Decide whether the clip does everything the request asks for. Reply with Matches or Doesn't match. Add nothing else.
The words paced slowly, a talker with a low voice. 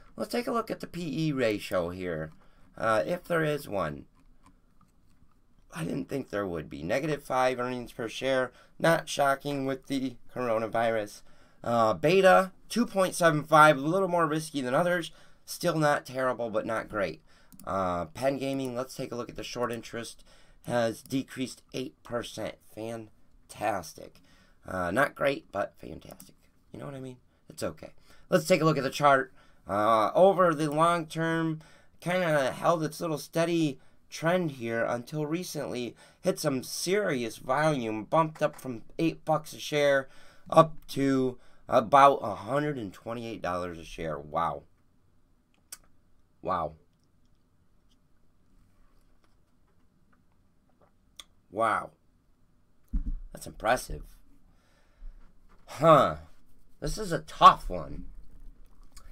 Matches